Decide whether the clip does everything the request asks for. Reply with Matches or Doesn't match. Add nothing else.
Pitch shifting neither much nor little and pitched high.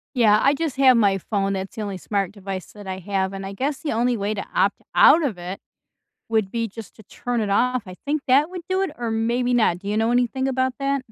Matches